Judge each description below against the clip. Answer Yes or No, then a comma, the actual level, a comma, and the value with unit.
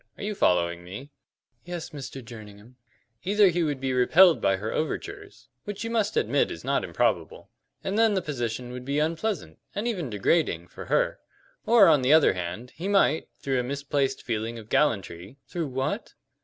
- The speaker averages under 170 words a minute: No, average, 185 wpm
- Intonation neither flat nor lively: No, wide, 7.7 semitones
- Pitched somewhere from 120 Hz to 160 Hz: Yes, medium, 140 Hz